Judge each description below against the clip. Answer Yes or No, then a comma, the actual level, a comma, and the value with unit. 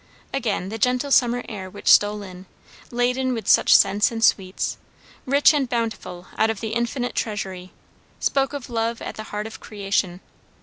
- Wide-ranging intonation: No, average, 3.5 semitones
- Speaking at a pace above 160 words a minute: Yes, average, 170 wpm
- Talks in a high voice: Yes, high, 225 Hz